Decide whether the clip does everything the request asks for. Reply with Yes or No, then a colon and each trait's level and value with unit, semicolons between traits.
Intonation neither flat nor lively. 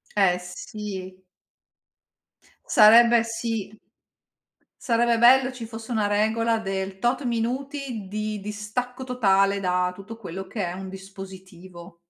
Yes: average, 3.4 semitones